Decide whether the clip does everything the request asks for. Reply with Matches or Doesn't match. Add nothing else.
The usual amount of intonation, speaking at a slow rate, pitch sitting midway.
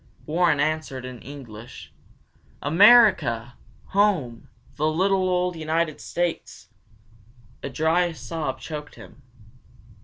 Matches